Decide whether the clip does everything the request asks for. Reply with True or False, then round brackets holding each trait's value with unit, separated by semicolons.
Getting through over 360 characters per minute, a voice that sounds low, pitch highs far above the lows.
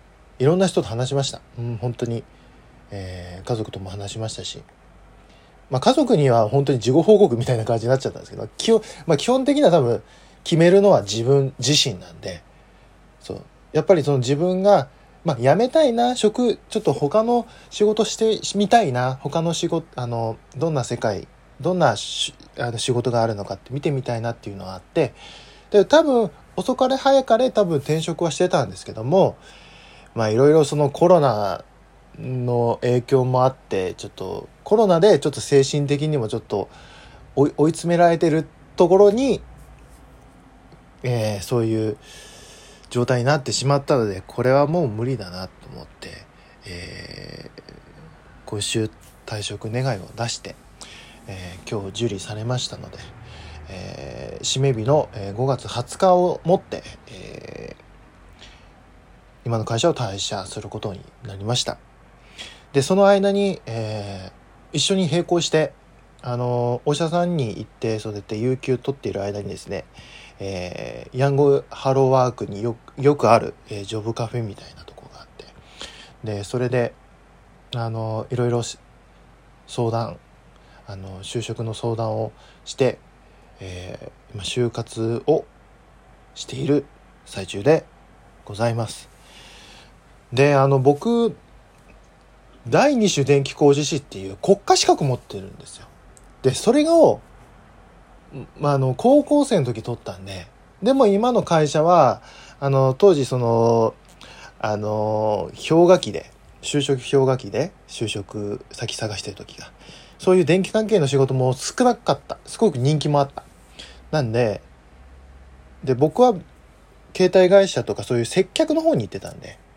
False (285 characters per minute; 130 Hz; 7.0 semitones)